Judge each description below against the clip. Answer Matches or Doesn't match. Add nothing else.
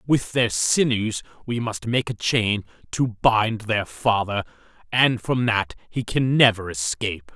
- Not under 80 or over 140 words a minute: Doesn't match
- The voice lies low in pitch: Matches